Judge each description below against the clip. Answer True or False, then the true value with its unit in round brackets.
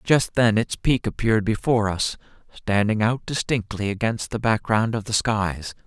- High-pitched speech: False (110 Hz)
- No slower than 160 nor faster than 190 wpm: True (165 wpm)